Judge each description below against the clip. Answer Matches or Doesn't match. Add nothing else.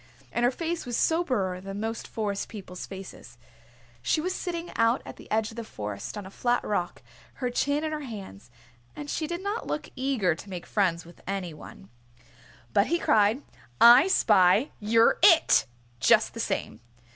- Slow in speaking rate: Doesn't match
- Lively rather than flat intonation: Matches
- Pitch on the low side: Doesn't match